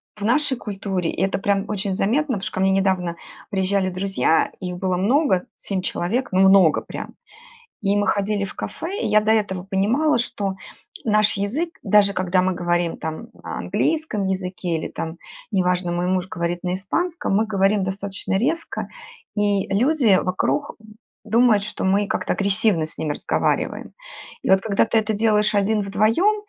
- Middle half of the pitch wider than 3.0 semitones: No, narrow, 2.6 semitones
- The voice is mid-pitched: No, high, 200 Hz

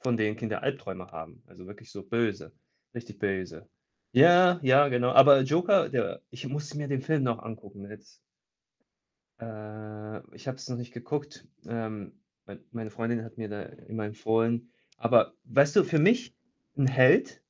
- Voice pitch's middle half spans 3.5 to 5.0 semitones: Yes, average, 4.5 semitones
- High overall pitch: No, low, 120 Hz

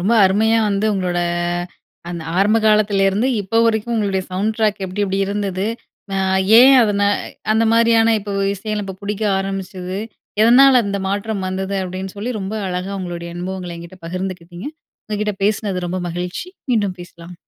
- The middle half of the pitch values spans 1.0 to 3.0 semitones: Yes, narrow, 2.6 semitones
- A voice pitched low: No, high, 195 Hz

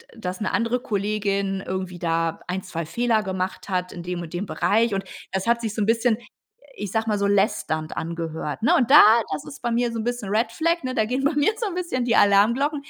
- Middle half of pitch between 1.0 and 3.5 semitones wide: No, average, 4.4 semitones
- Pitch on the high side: Yes, high, 210 Hz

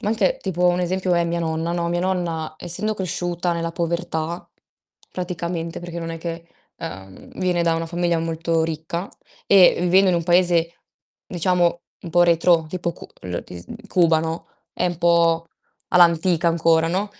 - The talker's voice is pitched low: No, medium, 170 Hz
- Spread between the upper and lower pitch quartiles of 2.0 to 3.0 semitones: No, narrow, 1.3 semitones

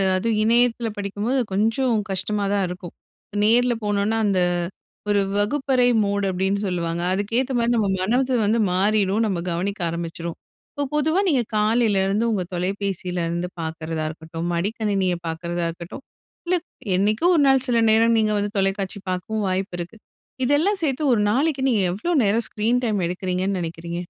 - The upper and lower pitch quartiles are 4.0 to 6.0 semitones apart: Yes, average, 4.3 semitones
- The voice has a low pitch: No, high, 205 Hz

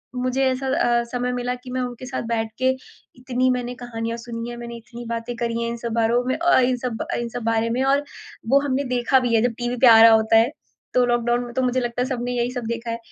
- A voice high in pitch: Yes, high, 240 Hz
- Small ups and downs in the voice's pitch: Yes, narrow, 1.4 semitones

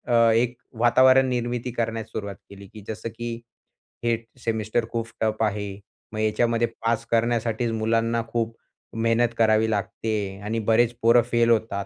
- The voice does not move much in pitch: Yes, narrow, 1.3 semitones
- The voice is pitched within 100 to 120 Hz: Yes, low, 115 Hz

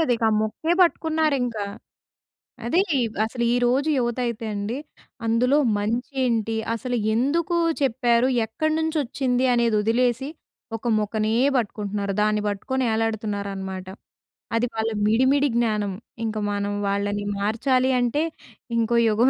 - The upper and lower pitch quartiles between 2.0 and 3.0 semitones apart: No, average, 3.4 semitones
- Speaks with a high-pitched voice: Yes, high, 235 Hz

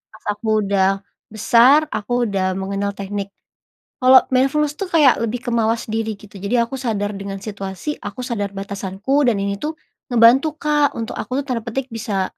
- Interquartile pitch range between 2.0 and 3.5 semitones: No, average, 4.4 semitones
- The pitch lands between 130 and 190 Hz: No, high, 220 Hz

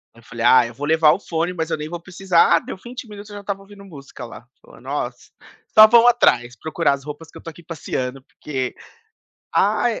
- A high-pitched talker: No, medium, 160 Hz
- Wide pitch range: Yes, wide, 6.2 semitones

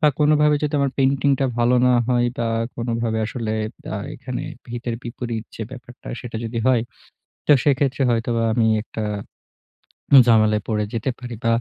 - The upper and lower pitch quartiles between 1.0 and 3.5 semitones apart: Yes, narrow, 2.5 semitones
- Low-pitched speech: Yes, low, 120 Hz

